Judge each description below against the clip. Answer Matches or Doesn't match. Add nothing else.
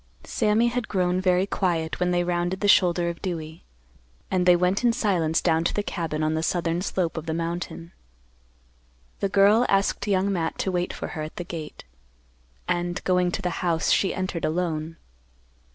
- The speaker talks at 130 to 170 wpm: Doesn't match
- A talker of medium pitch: Matches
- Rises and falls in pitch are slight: Matches